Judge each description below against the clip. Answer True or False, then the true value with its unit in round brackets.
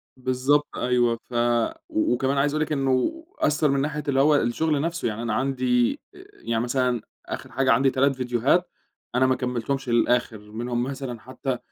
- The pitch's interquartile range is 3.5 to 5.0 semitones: False (2.8 semitones)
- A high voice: False (130 Hz)